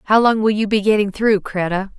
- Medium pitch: No, high, 205 Hz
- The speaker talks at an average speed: No, fast, 240 wpm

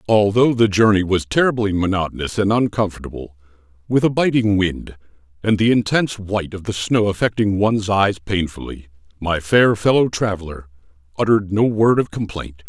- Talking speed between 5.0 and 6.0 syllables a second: Yes, 5.4 syllables/s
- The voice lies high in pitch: No, low, 100 Hz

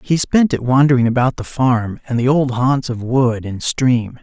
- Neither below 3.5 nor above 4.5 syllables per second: Yes, 4.4 syllables/s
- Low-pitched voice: Yes, low, 125 Hz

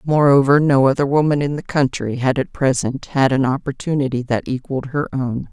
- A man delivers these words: No, female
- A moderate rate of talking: Yes, average, 185 wpm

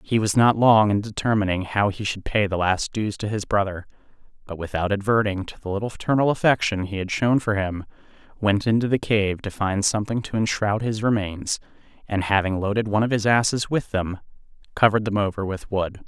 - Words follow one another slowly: No, average, 200 wpm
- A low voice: Yes, low, 105 Hz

